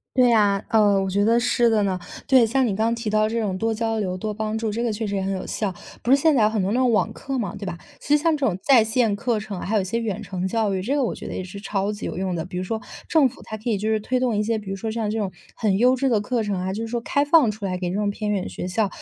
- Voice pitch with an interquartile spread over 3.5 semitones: No, average, 2.8 semitones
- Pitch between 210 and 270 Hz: Yes, high, 215 Hz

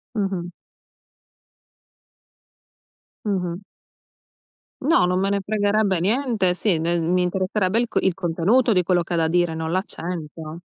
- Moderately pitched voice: Yes, medium, 180 Hz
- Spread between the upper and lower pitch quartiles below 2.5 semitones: No, average, 2.9 semitones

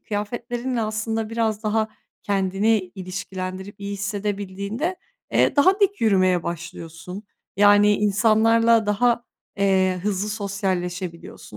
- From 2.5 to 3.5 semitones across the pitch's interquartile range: Yes, average, 2.9 semitones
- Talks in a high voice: Yes, high, 205 Hz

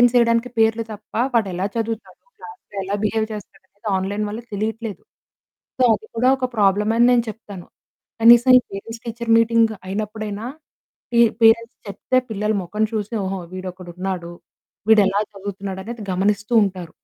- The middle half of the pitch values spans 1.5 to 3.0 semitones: Yes, average, 2.7 semitones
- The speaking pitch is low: No, high, 215 Hz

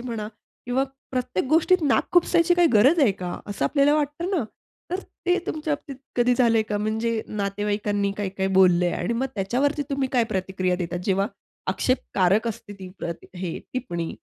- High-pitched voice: Yes, high, 225 Hz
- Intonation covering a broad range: Yes, wide, 6.2 semitones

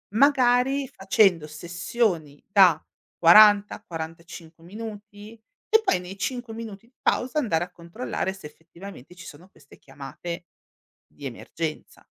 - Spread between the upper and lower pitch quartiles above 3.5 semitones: Yes, average, 5.2 semitones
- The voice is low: No, high, 190 Hz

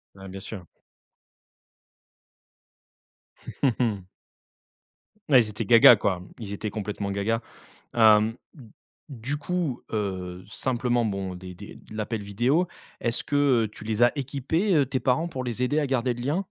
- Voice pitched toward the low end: Yes, low, 115 Hz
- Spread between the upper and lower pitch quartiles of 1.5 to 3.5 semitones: No, average, 4.4 semitones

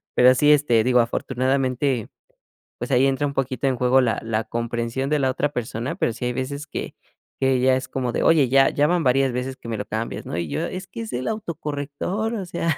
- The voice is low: Yes, low, 130 Hz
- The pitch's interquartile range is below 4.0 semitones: Yes, average, 3.0 semitones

